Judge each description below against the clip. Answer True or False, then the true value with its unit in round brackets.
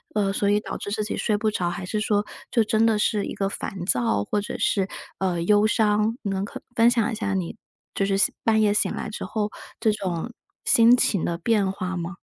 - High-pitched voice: True (205 Hz)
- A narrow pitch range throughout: True (2.2 semitones)